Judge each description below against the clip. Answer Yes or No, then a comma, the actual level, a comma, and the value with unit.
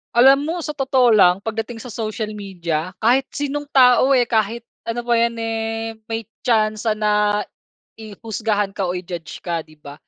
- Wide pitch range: No, average, 2.9 semitones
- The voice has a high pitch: Yes, high, 225 Hz